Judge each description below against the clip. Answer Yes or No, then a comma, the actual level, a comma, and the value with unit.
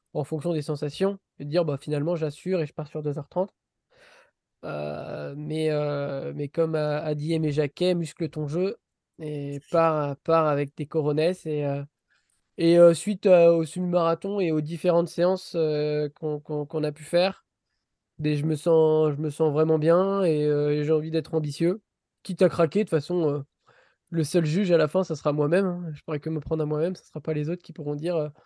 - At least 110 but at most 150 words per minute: No, average, 210 wpm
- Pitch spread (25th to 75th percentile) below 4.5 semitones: Yes, narrow, 2.5 semitones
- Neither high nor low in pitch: Yes, medium, 160 Hz